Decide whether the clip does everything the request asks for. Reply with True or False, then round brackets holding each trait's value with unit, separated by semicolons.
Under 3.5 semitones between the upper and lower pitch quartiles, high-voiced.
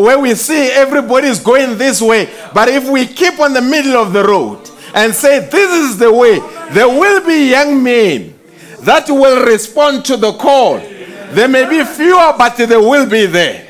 False (3.9 semitones; 265 Hz)